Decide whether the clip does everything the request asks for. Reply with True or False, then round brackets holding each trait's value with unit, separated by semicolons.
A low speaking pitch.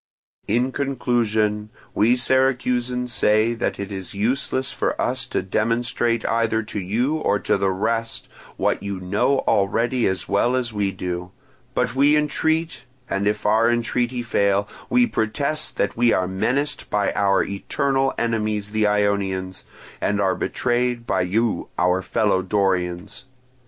True (110 Hz)